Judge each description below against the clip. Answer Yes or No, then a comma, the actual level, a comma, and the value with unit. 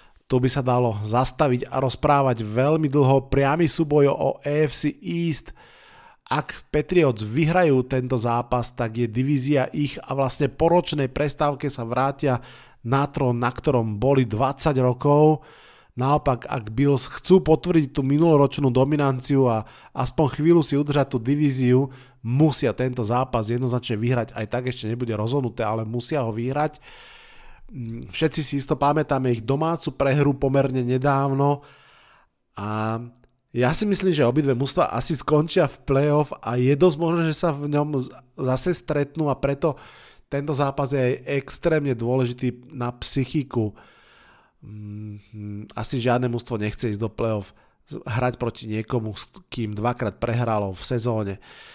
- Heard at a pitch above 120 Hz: Yes, low, 135 Hz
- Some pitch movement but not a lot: Yes, average, 3.4 semitones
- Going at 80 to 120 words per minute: No, average, 140 wpm